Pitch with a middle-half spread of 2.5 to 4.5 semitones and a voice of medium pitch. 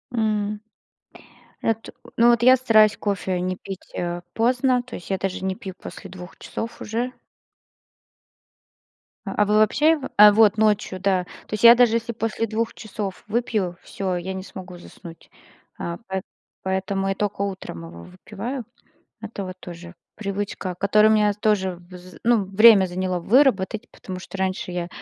No: average, 3.2 semitones; high, 200 Hz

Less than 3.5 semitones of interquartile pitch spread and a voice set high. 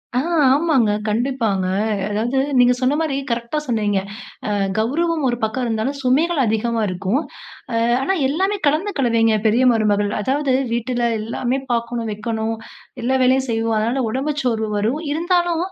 No: average, 3.9 semitones; high, 240 Hz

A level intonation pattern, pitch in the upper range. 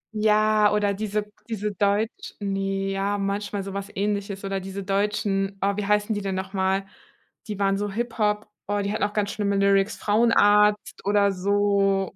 Yes: narrow, 1.1 semitones; high, 200 Hz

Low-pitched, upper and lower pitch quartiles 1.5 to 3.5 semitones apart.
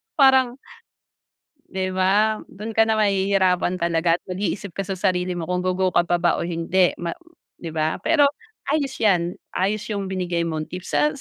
No: medium, 185 Hz; average, 2.8 semitones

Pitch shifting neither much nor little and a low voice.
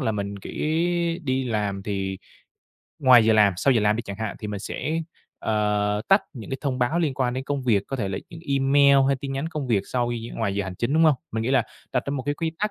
Yes: average, 4.9 semitones; low, 120 Hz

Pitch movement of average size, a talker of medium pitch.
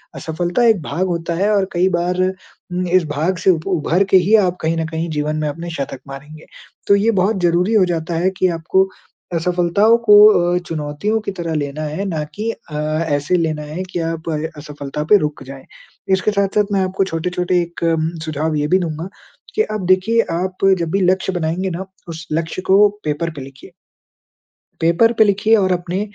Yes: average, 3.1 semitones; medium, 175 Hz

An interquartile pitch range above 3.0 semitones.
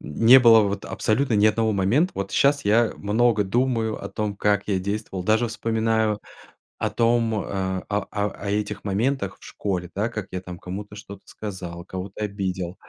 No: narrow, 2.6 semitones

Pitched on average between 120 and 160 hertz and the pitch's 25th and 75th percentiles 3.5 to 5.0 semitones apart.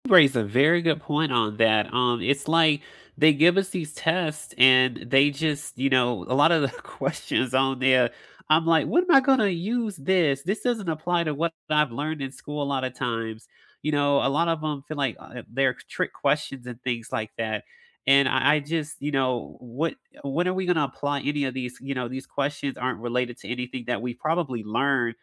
Yes: medium, 140 Hz; average, 4.0 semitones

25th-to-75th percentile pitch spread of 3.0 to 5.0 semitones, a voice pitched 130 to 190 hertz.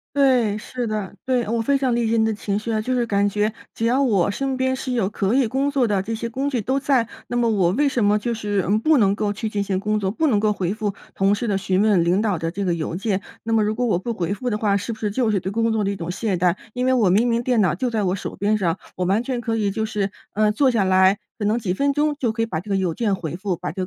No: average, 3.3 semitones; high, 215 Hz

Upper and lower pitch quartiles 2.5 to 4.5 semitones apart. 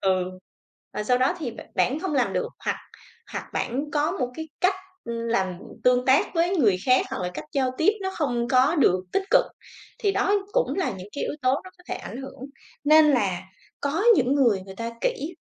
No: wide, 5.5 semitones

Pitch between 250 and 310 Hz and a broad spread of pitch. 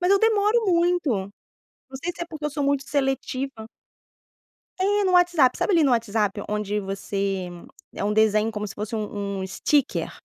Yes: very high, 255 Hz; wide, 8.7 semitones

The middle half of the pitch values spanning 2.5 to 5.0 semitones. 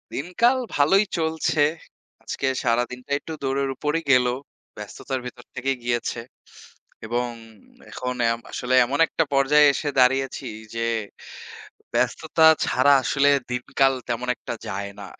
Yes: average, 2.8 semitones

